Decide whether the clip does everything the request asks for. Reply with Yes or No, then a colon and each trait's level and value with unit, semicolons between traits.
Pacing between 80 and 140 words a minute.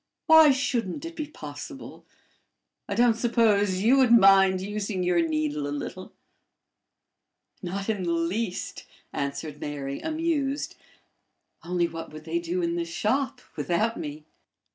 Yes: slow, 135 wpm